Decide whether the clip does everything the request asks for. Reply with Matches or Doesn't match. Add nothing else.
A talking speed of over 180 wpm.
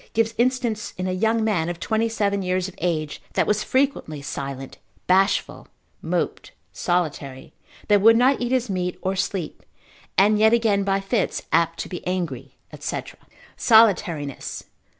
Doesn't match